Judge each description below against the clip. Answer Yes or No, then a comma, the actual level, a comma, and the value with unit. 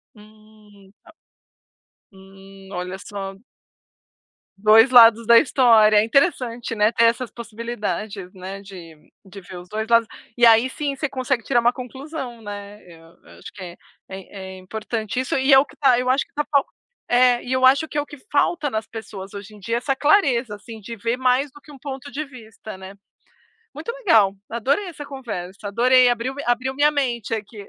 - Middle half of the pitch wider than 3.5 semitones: Yes, average, 4.2 semitones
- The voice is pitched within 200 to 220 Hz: No, high, 230 Hz